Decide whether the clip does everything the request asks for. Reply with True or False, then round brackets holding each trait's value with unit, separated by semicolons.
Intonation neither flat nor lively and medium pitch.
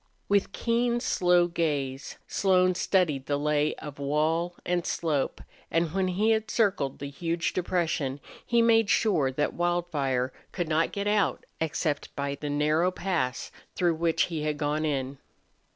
True (4.0 semitones; 165 Hz)